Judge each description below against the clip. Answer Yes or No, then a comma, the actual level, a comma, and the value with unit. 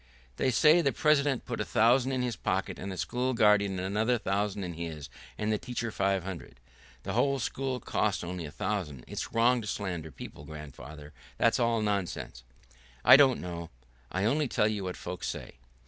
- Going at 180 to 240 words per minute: Yes, average, 185 wpm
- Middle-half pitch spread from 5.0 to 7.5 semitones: Yes, wide, 5.6 semitones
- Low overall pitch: Yes, low, 105 Hz